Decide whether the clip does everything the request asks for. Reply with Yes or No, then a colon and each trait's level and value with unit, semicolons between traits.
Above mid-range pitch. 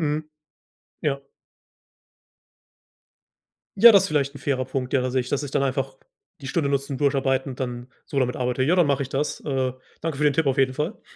No: medium, 140 Hz